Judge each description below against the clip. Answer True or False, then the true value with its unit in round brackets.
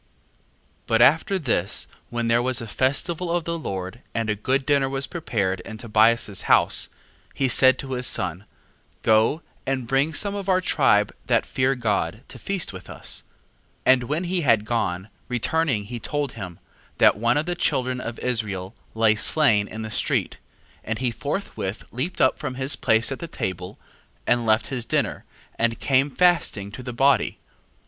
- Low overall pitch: True (125 Hz)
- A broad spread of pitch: False (4.5 semitones)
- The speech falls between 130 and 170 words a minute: False (180 wpm)